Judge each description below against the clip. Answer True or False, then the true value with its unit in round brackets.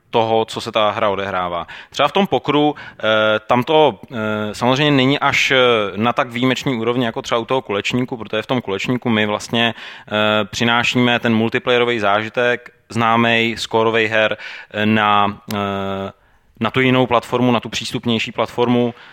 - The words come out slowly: False (145 wpm)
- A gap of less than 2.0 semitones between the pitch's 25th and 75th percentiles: False (2.7 semitones)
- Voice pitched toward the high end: False (115 Hz)